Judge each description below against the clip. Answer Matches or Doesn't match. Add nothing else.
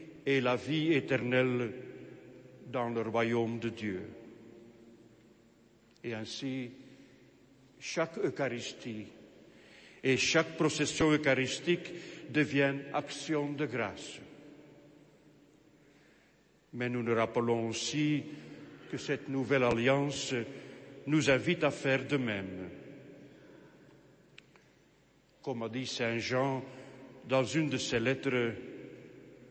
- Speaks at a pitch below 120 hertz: Doesn't match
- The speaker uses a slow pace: Matches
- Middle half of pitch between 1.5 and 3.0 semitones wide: Doesn't match